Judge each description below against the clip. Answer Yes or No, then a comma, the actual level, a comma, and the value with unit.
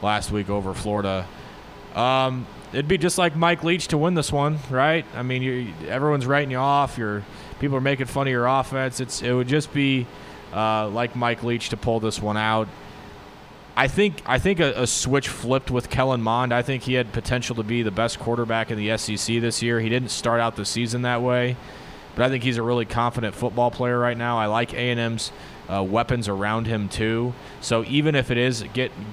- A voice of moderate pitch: No, low, 120 Hz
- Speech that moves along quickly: Yes, fast, 210 wpm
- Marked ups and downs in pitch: No, average, 2.8 semitones